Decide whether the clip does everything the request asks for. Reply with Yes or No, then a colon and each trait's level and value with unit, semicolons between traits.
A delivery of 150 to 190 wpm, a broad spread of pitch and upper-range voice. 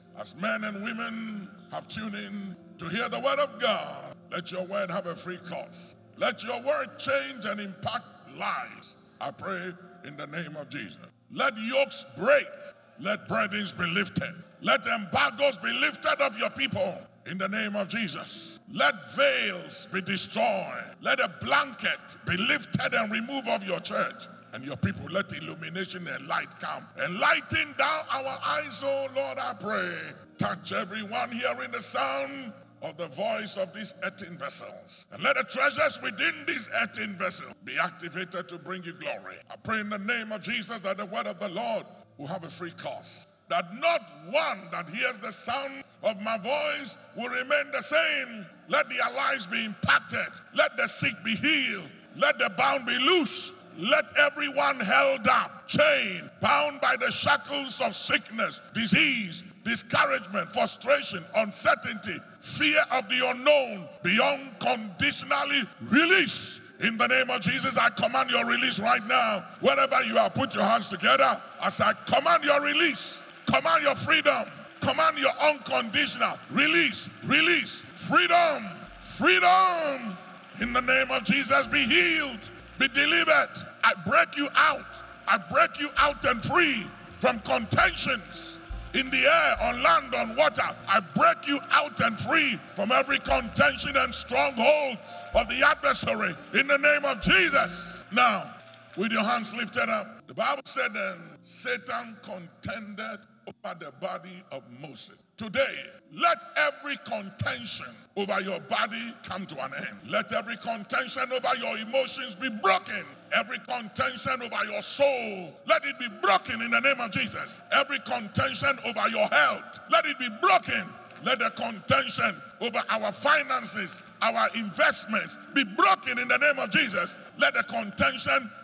Yes: average, 155 wpm; wide, 6.3 semitones; high, 235 Hz